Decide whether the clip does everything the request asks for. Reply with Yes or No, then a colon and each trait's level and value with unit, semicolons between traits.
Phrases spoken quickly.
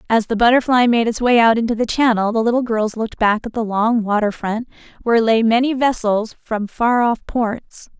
Yes: fast, 210 wpm